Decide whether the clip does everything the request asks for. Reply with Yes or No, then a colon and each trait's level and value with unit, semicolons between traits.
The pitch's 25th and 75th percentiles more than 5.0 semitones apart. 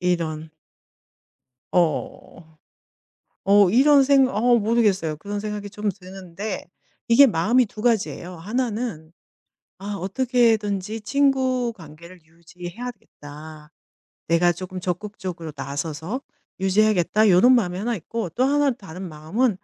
Yes: wide, 5.4 semitones